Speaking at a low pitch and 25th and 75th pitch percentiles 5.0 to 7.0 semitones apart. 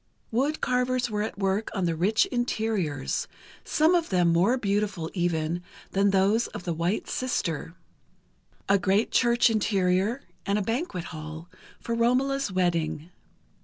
No: high, 200 Hz; average, 5.3 semitones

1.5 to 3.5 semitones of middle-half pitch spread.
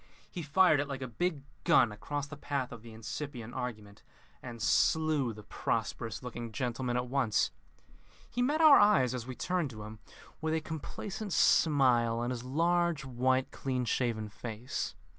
No: average, 4.7 semitones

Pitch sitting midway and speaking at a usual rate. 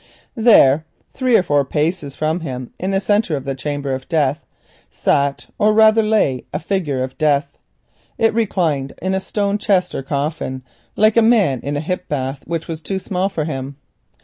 Yes: medium, 160 Hz; average, 185 wpm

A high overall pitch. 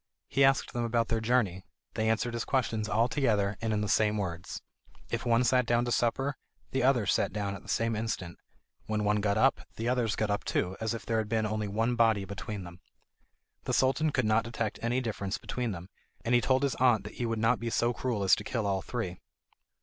No: low, 115 Hz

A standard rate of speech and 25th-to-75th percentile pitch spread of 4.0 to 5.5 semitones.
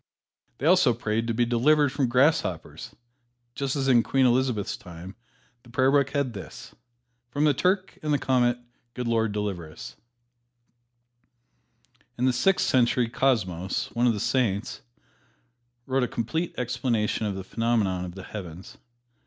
Yes: average, 150 wpm; average, 4.3 semitones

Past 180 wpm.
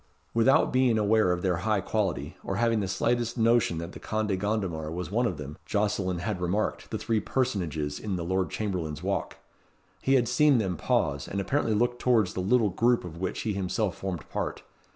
Yes: average, 195 wpm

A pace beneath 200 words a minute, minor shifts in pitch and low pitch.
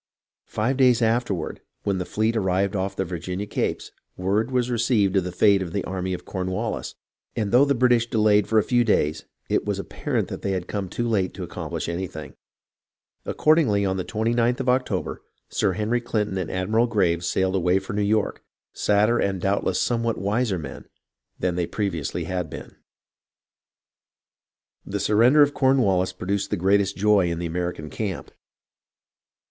No: average, 170 wpm; average, 3.9 semitones; low, 100 Hz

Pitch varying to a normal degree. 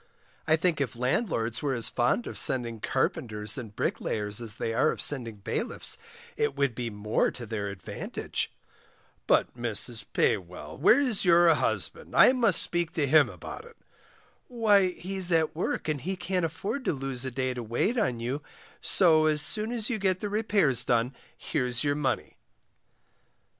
No: wide, 7.8 semitones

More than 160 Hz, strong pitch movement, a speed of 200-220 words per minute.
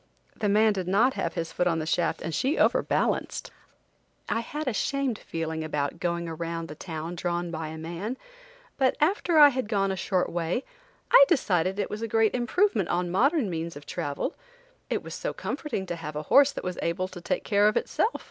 Yes: medium, 185 Hz; wide, 6.4 semitones; fast, 205 wpm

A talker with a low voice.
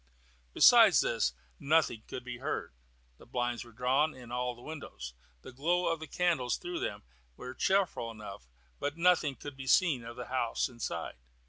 Yes: low, 130 Hz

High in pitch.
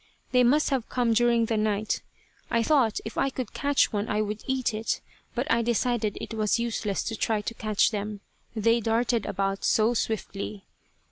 Yes: high, 225 Hz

